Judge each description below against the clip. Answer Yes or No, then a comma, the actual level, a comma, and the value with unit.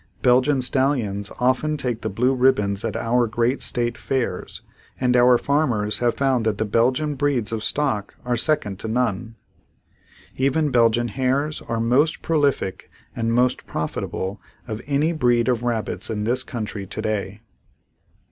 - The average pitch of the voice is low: Yes, low, 120 Hz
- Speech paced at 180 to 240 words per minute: No, average, 145 wpm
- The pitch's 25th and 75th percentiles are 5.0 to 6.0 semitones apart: No, average, 3.3 semitones